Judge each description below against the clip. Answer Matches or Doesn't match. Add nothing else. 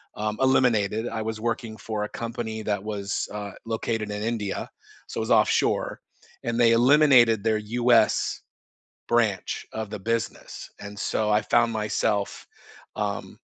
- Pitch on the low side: Matches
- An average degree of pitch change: Doesn't match